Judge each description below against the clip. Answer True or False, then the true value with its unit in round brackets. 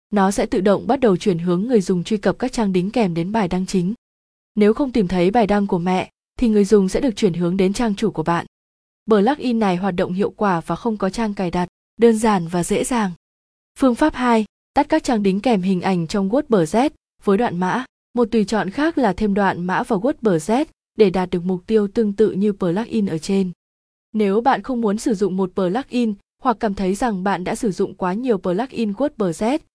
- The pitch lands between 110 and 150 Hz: False (210 Hz)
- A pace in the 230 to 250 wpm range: True (240 wpm)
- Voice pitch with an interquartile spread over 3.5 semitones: True (3.9 semitones)